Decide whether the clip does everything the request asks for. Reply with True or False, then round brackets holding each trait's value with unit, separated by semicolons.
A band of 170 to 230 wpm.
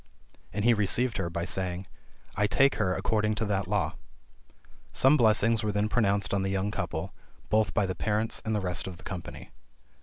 True (190 wpm)